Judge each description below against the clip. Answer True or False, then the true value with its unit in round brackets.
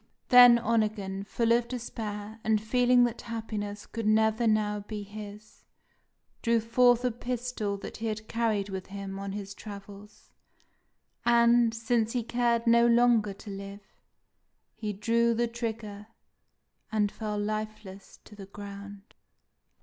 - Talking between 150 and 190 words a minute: False (135 wpm)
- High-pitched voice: True (220 Hz)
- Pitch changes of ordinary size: False (2.2 semitones)